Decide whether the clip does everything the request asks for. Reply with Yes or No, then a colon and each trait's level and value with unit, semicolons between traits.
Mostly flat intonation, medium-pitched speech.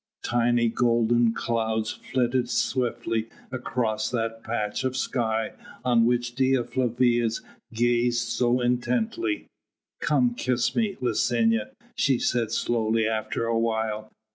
No: narrow, 1.6 semitones; low, 120 Hz